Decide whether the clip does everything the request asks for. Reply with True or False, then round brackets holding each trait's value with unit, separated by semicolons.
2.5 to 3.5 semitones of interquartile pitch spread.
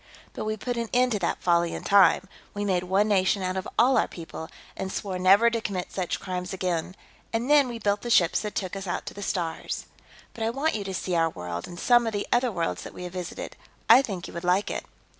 False (3.9 semitones)